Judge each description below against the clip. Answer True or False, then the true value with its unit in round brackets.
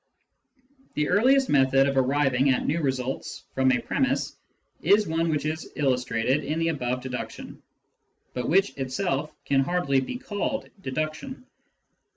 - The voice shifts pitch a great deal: False (4.1 semitones)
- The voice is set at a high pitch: False (145 Hz)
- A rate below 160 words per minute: True (140 wpm)